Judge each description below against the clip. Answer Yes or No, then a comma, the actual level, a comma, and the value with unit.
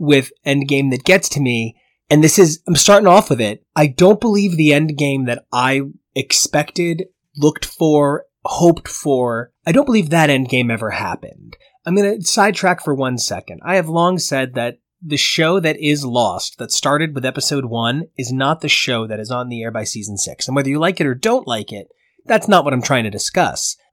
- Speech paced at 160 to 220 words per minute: Yes, fast, 205 wpm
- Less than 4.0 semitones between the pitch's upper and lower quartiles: No, average, 5.2 semitones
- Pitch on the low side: No, medium, 145 Hz